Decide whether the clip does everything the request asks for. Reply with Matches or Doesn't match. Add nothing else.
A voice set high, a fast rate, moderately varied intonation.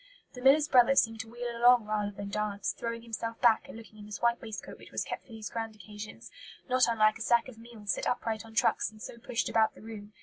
Doesn't match